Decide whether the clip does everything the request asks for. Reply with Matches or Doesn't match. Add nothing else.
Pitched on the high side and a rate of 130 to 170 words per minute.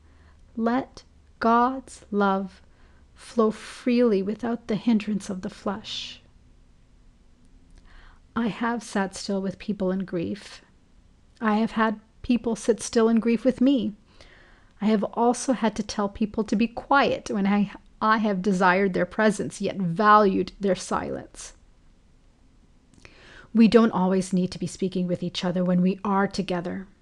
Matches